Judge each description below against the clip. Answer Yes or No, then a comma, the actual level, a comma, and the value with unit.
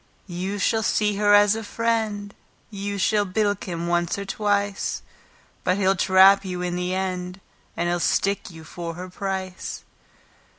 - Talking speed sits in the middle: Yes, average, 160 wpm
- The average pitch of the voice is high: Yes, high, 195 Hz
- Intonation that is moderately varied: No, narrow, 2.1 semitones